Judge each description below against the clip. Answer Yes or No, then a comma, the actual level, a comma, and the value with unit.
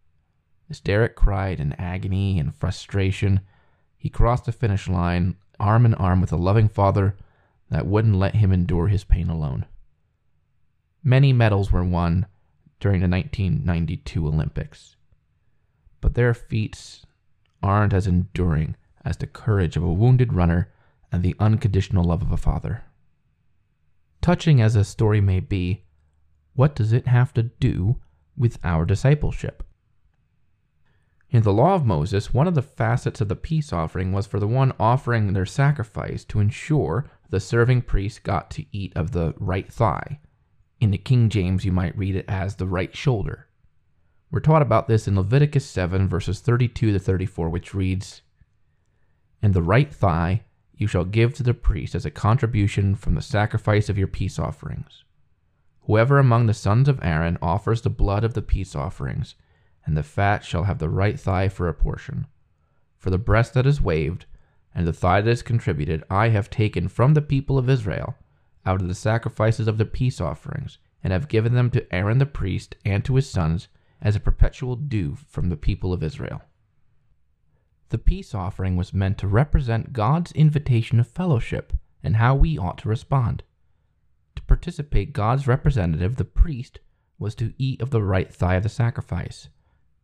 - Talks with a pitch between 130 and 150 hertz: No, low, 100 Hz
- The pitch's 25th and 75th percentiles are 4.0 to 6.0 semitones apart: Yes, average, 4.8 semitones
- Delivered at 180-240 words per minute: No, average, 170 wpm